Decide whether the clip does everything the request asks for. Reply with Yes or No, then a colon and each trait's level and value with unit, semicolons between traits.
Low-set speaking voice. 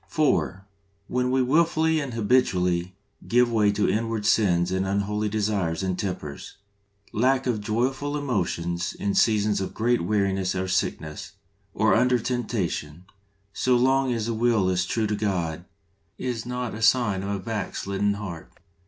Yes: low, 105 Hz